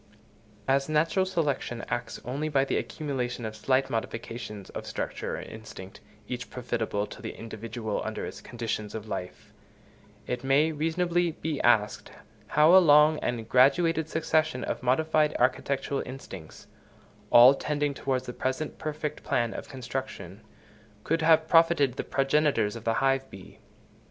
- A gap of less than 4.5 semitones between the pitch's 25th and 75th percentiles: No, average, 4.8 semitones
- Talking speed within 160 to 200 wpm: No, average, 145 wpm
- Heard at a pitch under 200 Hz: Yes, low, 135 Hz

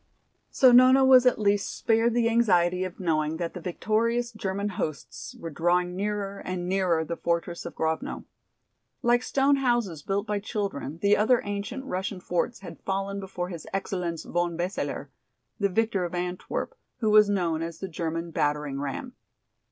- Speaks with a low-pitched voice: No, high, 190 Hz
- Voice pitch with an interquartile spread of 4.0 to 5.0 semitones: Yes, average, 4.3 semitones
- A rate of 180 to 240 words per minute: No, average, 165 wpm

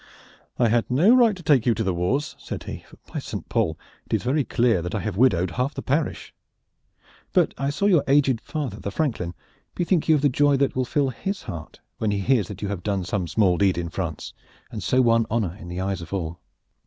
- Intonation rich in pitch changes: Yes, wide, 7.1 semitones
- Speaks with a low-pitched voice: Yes, low, 115 Hz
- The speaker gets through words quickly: Yes, fast, 235 wpm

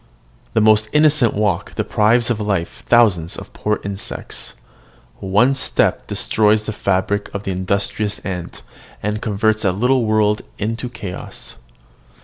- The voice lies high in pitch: No, low, 105 Hz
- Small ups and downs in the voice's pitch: Yes, narrow, 2.1 semitones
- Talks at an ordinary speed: No, slow, 130 wpm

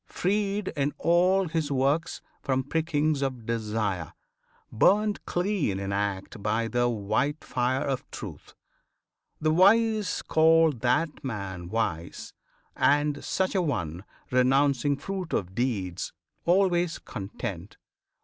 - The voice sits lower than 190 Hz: Yes, medium, 140 Hz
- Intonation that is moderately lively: No, wide, 7.4 semitones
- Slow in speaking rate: Yes, slow, 115 wpm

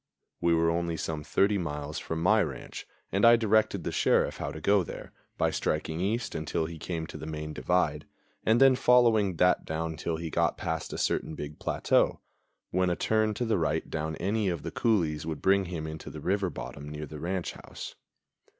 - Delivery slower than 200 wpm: No, fast, 205 wpm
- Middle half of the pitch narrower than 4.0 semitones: No, average, 4.4 semitones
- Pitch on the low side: Yes, very low, 85 Hz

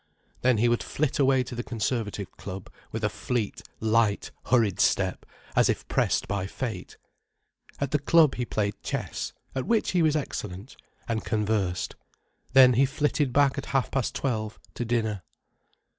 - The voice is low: Yes, low, 120 Hz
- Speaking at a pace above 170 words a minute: No, average, 155 wpm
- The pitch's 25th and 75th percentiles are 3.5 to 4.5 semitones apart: Yes, average, 4.0 semitones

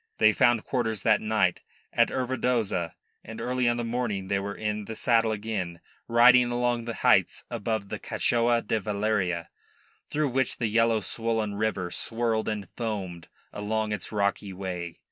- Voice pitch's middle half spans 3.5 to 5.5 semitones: No, average, 2.7 semitones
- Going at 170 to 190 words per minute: No, average, 160 wpm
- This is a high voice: No, low, 110 Hz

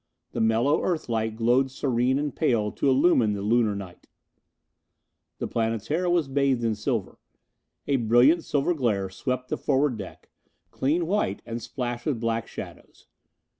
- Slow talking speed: No, average, 150 wpm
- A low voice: Yes, low, 120 Hz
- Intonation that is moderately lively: Yes, average, 3.9 semitones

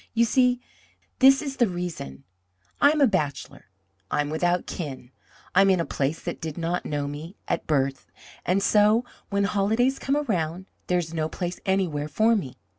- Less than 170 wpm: No, average, 185 wpm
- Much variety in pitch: Yes, wide, 6.1 semitones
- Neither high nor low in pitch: Yes, medium, 180 Hz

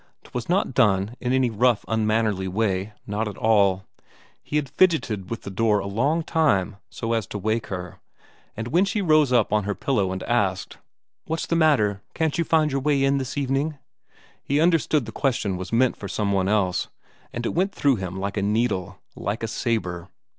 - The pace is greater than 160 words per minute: Yes, average, 195 wpm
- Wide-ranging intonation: Yes, wide, 5.9 semitones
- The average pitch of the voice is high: No, low, 115 Hz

